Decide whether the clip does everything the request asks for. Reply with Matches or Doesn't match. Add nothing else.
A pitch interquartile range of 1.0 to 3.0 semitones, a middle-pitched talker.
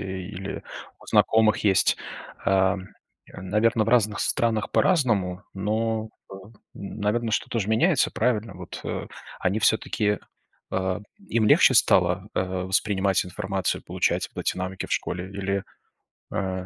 Doesn't match